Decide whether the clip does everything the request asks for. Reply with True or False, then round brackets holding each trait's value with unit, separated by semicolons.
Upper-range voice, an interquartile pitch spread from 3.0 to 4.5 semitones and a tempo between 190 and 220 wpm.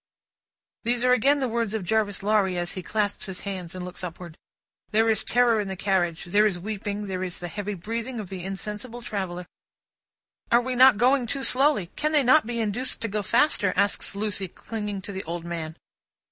True (210 Hz; 4.0 semitones; 200 wpm)